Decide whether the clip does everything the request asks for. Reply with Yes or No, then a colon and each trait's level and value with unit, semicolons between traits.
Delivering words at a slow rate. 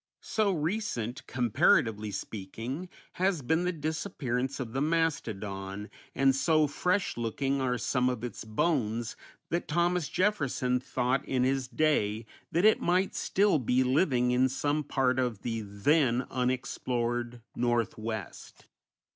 Yes: slow, 130 wpm